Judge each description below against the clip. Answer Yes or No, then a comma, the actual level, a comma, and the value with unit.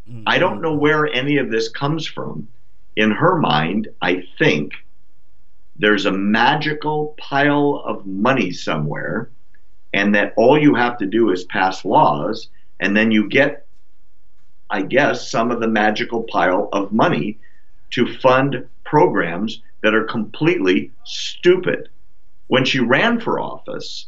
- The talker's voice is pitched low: Yes, low, 115 Hz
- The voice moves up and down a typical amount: No, wide, 5.9 semitones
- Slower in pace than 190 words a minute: Yes, average, 140 wpm